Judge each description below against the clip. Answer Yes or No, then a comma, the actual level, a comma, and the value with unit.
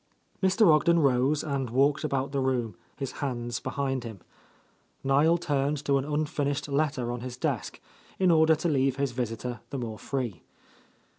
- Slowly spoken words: No, average, 160 wpm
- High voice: No, medium, 140 Hz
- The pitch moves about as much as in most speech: Yes, average, 3.0 semitones